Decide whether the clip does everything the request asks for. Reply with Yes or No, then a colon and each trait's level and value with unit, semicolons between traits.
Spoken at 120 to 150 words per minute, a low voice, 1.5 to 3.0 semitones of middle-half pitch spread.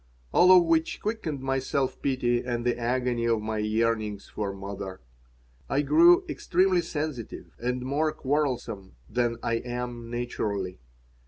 No: average, 140 wpm; low, 125 Hz; average, 4.3 semitones